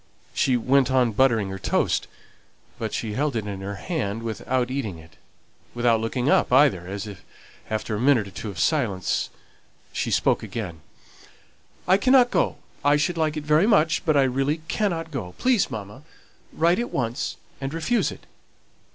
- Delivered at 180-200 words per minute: No, average, 170 wpm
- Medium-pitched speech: No, low, 130 Hz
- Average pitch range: No, wide, 6.2 semitones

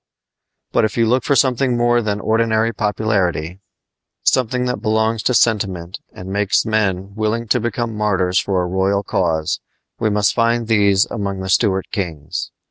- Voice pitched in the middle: No, low, 105 Hz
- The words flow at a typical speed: Yes, average, 160 wpm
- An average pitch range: Yes, average, 3.2 semitones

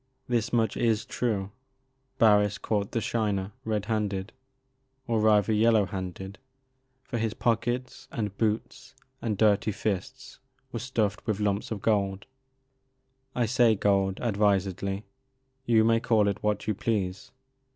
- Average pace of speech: No, slow, 130 wpm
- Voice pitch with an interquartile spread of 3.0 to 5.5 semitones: No, narrow, 2.4 semitones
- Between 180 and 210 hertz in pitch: No, low, 105 Hz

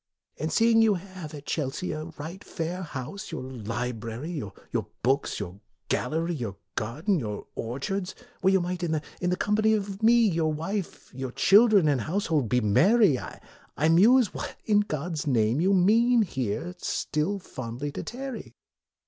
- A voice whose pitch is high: No, medium, 165 Hz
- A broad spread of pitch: Yes, wide, 7.1 semitones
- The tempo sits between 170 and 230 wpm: No, average, 155 wpm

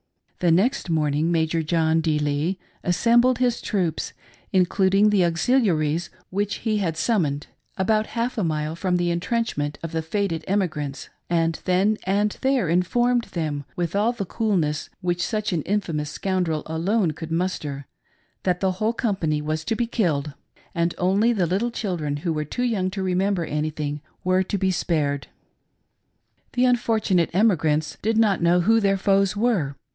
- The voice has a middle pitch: Yes, medium, 180 Hz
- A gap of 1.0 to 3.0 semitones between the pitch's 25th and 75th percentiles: No, average, 4.6 semitones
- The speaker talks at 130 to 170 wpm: Yes, average, 165 wpm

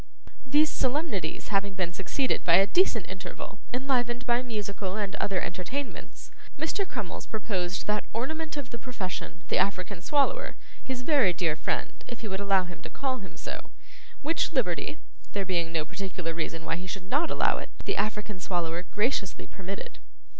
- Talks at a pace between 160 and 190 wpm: Yes, average, 170 wpm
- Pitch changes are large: Yes, wide, 5.8 semitones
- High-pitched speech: Yes, high, 200 Hz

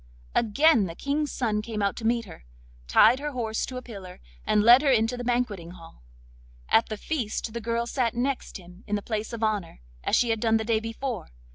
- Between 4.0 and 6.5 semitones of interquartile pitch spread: No, average, 2.7 semitones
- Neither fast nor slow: No, fast, 220 wpm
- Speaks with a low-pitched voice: No, high, 225 Hz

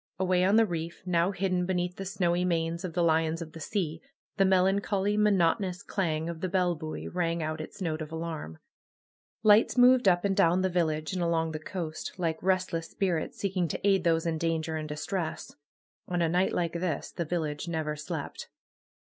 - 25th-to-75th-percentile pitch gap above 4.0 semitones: No, average, 2.7 semitones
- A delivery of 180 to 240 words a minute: Yes, average, 190 wpm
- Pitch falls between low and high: Yes, medium, 175 Hz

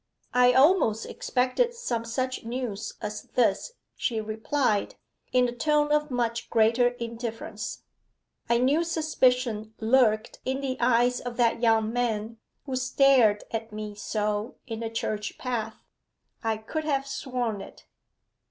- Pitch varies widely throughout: No, average, 2.8 semitones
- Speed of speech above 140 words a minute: No, slow, 135 wpm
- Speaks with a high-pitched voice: Yes, high, 240 Hz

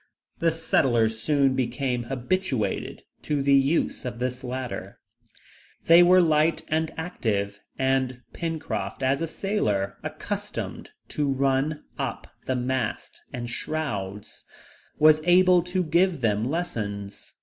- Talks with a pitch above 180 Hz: No, low, 135 Hz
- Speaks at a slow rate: Yes, slow, 120 wpm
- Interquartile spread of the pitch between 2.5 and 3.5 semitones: No, average, 5.2 semitones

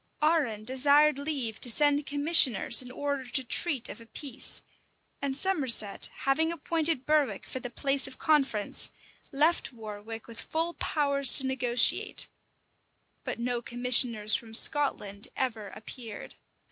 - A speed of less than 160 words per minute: Yes, slow, 135 wpm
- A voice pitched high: Yes, very high, 265 Hz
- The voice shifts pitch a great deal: No, average, 3.9 semitones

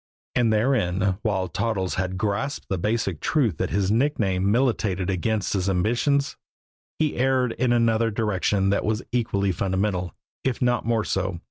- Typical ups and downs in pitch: Yes, average, 3.8 semitones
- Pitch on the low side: Yes, low, 105 Hz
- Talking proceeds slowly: No, average, 150 wpm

